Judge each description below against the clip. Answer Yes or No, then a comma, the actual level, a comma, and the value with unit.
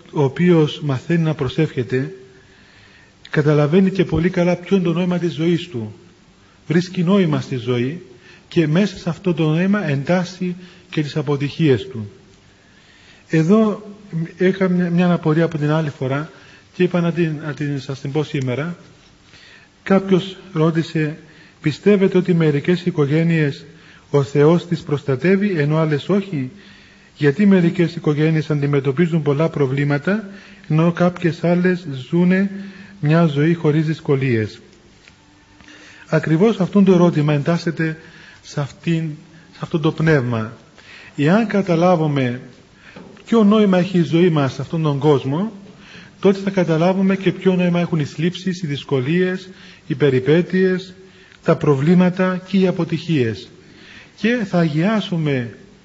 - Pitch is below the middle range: No, medium, 165 Hz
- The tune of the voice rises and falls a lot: No, average, 3.9 semitones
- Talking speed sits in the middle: Yes, average, 130 wpm